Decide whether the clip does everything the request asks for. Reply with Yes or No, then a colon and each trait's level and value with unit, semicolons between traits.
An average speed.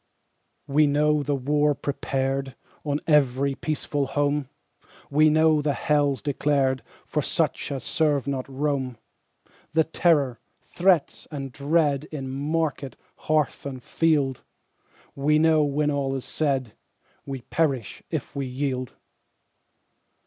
No: slow, 120 wpm